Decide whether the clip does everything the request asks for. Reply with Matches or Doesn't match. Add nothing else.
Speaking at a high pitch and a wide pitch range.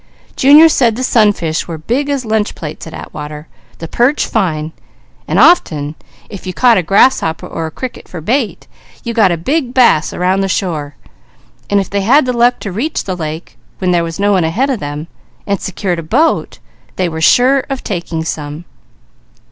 Matches